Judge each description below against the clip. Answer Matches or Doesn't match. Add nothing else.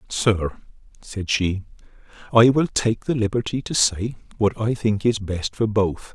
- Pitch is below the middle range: Matches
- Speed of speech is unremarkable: Matches